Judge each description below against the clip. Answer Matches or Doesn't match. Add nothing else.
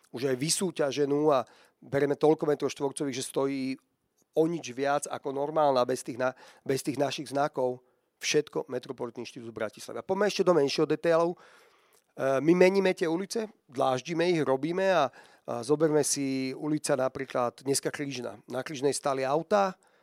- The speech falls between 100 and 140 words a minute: Doesn't match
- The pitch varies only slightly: Doesn't match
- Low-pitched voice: Doesn't match